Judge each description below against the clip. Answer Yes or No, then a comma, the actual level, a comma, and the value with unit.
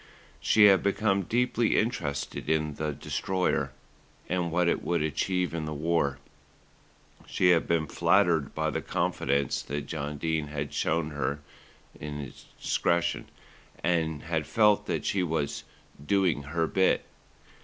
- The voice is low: Yes, very low, 80 Hz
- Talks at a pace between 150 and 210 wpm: No, slow, 135 wpm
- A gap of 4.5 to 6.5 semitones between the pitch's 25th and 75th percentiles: No, average, 3.7 semitones